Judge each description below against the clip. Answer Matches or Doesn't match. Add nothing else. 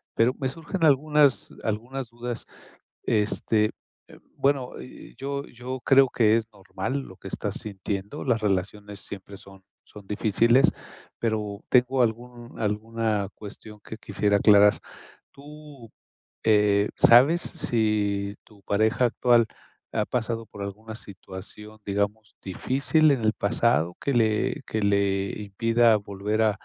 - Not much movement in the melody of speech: Doesn't match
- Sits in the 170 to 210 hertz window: Doesn't match